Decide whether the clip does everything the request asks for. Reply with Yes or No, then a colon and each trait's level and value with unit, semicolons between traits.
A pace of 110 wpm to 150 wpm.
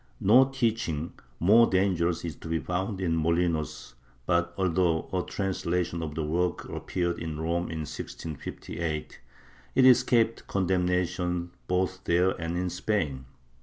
Yes: slow, 135 wpm